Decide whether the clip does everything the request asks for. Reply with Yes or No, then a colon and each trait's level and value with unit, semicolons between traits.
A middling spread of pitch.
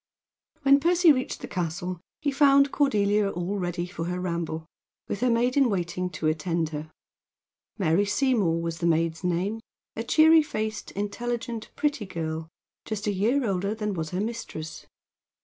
No: wide, 6.0 semitones